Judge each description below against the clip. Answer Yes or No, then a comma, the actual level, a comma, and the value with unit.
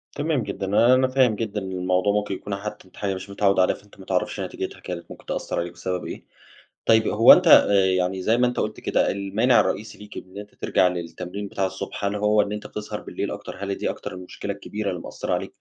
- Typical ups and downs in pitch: No, narrow, 2.3 semitones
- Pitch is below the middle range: Yes, low, 100 Hz